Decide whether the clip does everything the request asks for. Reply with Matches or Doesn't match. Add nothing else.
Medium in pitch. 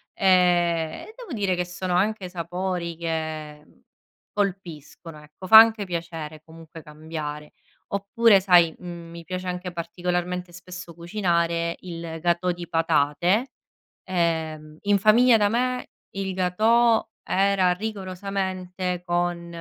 Matches